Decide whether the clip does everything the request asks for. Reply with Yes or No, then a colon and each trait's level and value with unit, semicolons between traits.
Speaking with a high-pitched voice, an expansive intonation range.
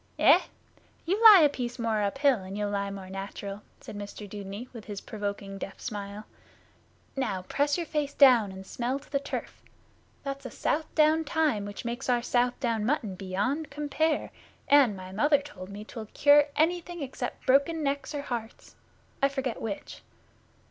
Yes: high, 245 Hz; wide, 6.0 semitones